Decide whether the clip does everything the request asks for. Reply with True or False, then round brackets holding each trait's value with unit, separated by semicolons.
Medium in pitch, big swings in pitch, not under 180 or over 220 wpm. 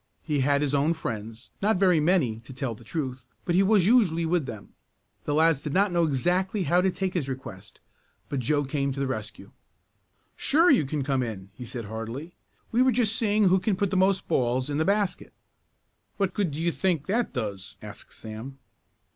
True (150 Hz; 6.7 semitones; 200 wpm)